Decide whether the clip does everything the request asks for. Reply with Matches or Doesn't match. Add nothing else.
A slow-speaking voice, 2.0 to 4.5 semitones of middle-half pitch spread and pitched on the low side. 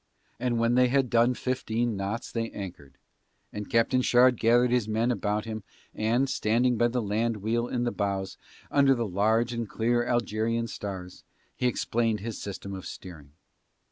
Doesn't match